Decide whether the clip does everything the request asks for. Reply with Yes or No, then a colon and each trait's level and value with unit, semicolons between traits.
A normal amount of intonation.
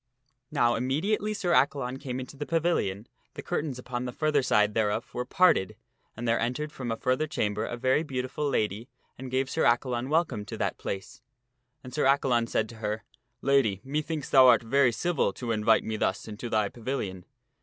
Yes: average, 4.0 semitones